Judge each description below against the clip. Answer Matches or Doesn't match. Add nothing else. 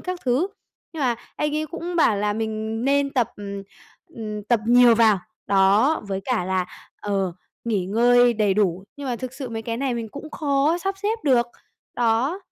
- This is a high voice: Matches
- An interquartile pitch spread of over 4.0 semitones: Matches